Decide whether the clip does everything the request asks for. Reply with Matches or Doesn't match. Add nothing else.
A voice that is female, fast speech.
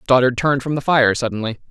Doesn't match